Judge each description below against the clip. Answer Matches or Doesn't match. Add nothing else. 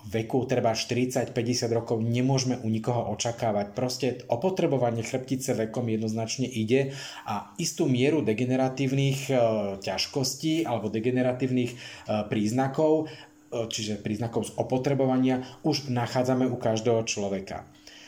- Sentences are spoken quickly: Doesn't match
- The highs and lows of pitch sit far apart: Doesn't match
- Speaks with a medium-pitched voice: Doesn't match